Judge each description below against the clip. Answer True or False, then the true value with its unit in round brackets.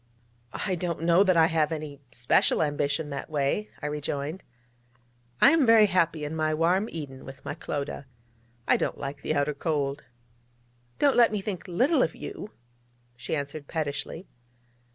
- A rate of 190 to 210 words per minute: False (160 wpm)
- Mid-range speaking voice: True (155 Hz)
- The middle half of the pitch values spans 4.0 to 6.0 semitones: True (4.3 semitones)